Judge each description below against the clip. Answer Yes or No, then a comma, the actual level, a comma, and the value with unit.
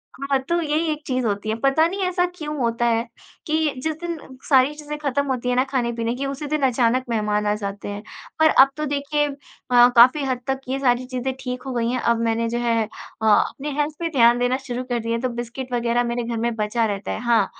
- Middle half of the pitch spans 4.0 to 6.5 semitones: No, average, 3.3 semitones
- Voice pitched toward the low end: No, very high, 250 Hz